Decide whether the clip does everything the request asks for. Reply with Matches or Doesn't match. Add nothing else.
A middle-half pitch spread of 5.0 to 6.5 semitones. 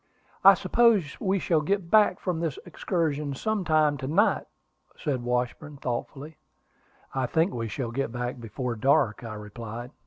Matches